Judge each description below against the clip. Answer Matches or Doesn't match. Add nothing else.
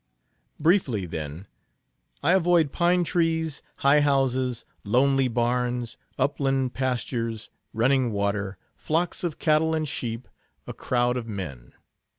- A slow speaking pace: Matches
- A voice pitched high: Doesn't match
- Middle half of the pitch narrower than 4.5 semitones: Doesn't match